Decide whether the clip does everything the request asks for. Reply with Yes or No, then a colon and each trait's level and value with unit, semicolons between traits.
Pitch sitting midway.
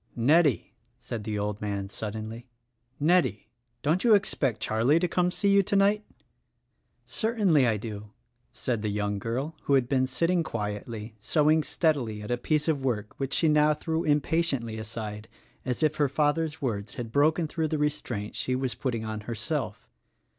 No: low, 130 Hz